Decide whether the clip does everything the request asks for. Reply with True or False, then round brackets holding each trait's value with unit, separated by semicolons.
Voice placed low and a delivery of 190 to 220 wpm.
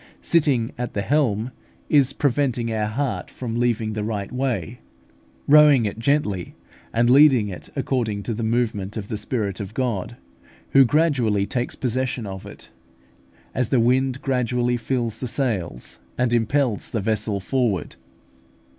False (120 Hz; 145 wpm)